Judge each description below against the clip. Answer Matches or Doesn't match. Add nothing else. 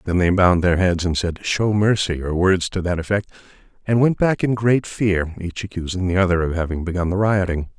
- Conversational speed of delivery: Doesn't match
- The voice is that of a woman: Doesn't match